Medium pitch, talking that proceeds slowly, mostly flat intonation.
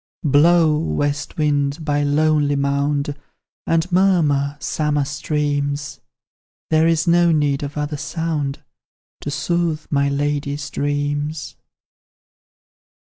Yes: medium, 145 Hz; slow, 105 wpm; narrow, 1.6 semitones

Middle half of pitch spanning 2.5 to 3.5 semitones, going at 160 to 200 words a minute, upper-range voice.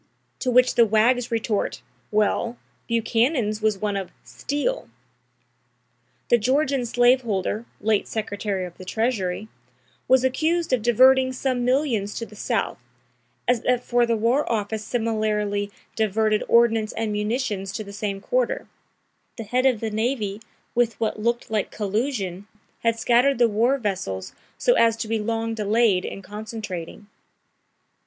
No: average, 2.8 semitones; average, 145 wpm; high, 225 Hz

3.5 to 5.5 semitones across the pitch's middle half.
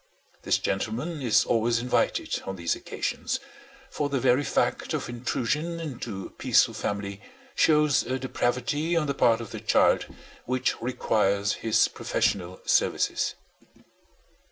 Yes: average, 4.5 semitones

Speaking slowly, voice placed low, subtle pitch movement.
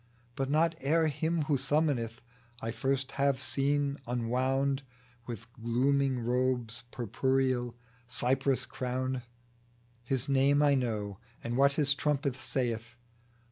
Yes: slow, 115 wpm; low, 130 Hz; narrow, 2.3 semitones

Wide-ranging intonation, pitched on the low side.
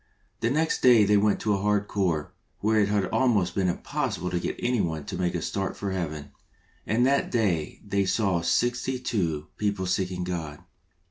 No: average, 3.7 semitones; low, 100 Hz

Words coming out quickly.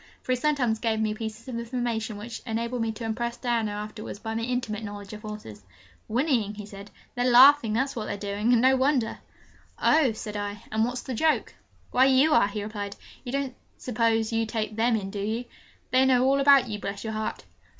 Yes: fast, 210 wpm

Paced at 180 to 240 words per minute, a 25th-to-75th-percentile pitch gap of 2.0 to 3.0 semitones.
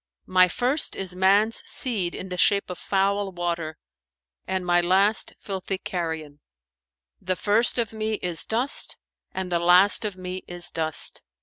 No: average, 150 wpm; narrow, 2.6 semitones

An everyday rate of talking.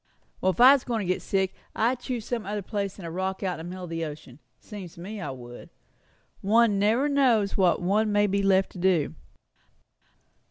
No: fast, 215 wpm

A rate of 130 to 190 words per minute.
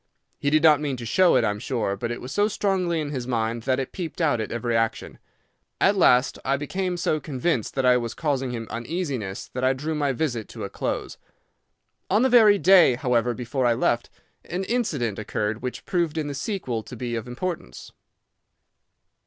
No: average, 200 wpm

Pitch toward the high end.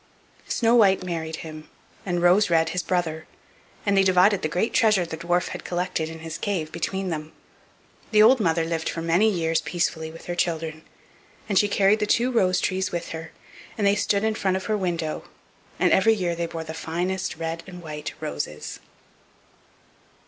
No: medium, 175 Hz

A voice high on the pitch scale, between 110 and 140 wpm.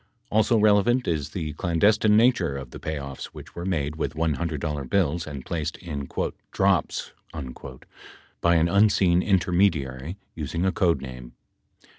No: very low, 85 Hz; slow, 135 wpm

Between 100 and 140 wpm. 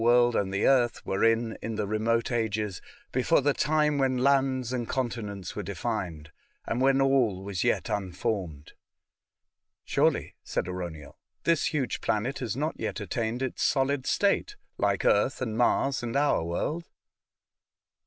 No: average, 160 wpm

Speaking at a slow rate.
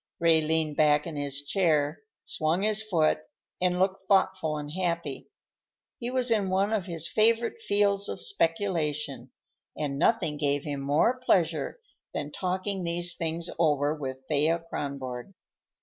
No: average, 145 wpm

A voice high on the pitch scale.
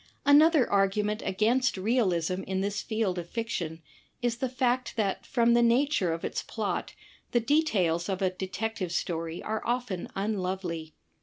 Yes: high, 210 Hz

